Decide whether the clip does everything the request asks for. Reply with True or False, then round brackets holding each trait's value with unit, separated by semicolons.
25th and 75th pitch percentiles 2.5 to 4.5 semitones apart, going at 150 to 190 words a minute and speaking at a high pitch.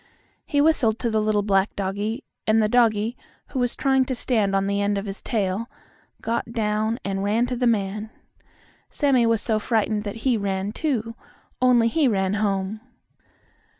True (2.8 semitones; 175 wpm; 220 Hz)